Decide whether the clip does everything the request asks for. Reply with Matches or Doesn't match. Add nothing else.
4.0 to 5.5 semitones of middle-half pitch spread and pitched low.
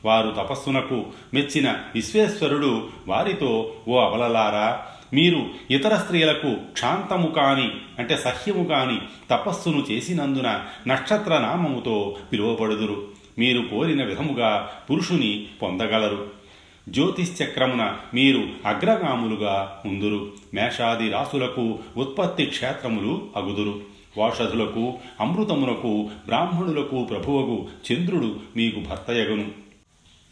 Matches